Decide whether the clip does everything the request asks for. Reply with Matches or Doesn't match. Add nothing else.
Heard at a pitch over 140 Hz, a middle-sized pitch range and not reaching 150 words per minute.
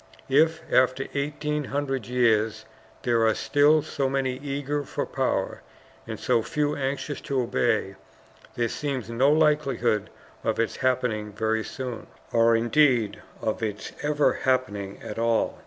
Doesn't match